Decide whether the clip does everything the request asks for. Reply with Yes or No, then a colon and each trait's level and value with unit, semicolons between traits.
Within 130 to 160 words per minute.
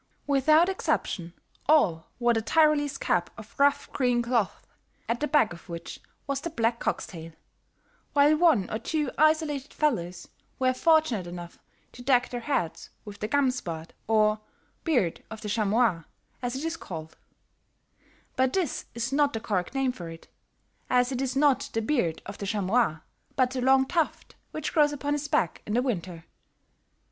No: average, 170 wpm